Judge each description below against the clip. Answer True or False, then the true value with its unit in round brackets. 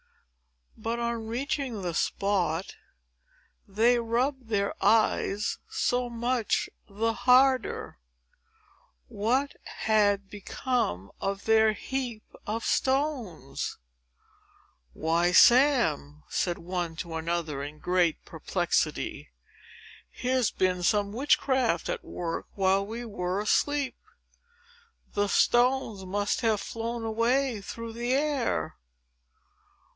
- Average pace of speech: False (100 wpm)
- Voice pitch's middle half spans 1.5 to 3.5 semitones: False (4.6 semitones)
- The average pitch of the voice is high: True (220 Hz)